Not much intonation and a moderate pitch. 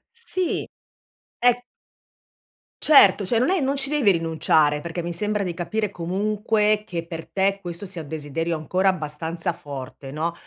No: average, 4.5 semitones; medium, 180 Hz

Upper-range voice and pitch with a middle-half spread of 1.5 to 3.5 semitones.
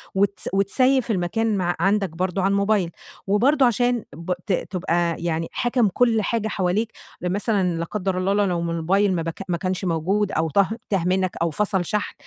Yes: high, 195 Hz; average, 3.2 semitones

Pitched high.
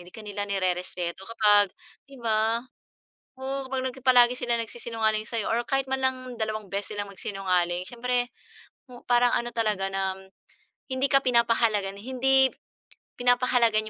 Yes: high, 230 Hz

